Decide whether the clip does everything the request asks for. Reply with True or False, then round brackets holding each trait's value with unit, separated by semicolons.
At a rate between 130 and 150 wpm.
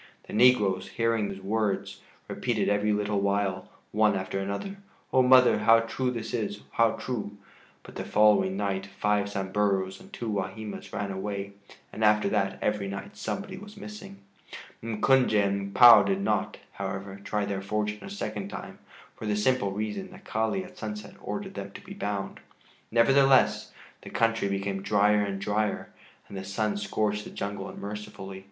False (165 wpm)